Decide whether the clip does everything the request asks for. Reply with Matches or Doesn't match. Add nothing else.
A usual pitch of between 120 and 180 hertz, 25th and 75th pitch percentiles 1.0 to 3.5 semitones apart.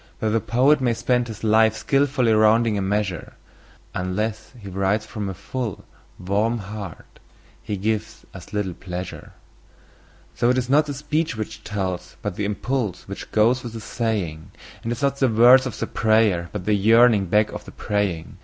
Doesn't match